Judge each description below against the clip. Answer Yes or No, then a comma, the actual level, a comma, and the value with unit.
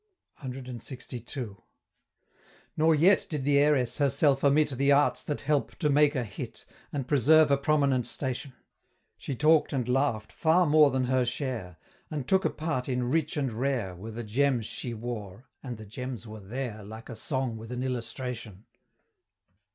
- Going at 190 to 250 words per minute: No, average, 165 wpm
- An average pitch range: Yes, average, 3.6 semitones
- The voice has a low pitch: Yes, low, 130 Hz